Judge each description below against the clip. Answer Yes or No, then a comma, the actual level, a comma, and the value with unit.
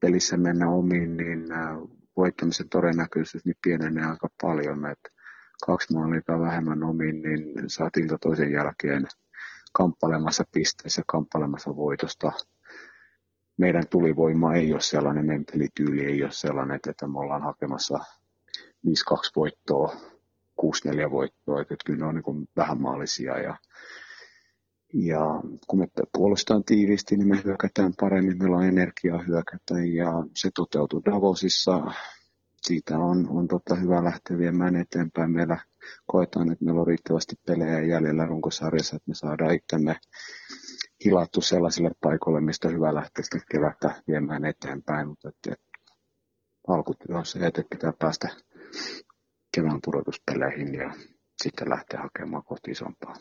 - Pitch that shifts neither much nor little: No, narrow, 2.1 semitones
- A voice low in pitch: Yes, very low, 80 Hz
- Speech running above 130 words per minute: No, average, 125 wpm